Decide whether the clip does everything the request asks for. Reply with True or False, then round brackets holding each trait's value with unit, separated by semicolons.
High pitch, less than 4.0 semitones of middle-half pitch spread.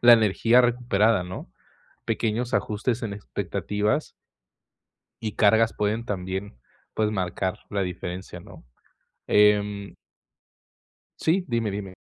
False (105 Hz; 2.6 semitones)